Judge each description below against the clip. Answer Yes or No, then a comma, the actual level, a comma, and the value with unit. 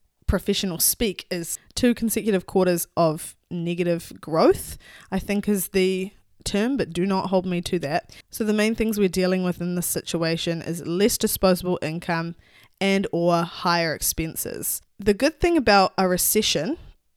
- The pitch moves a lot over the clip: No, average, 3.1 semitones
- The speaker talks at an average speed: Yes, average, 155 wpm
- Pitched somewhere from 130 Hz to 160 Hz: No, medium, 185 Hz